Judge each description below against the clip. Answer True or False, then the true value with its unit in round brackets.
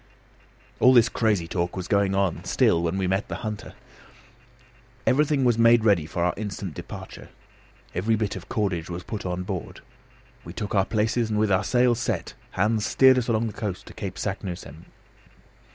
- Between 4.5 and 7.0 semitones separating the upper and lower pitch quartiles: False (3.7 semitones)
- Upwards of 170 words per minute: True (180 wpm)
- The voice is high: False (100 Hz)